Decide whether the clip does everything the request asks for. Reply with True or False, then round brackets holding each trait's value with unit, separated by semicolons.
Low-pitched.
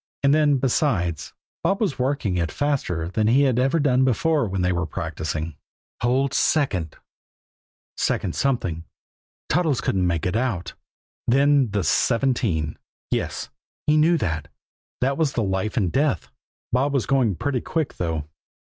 True (125 Hz)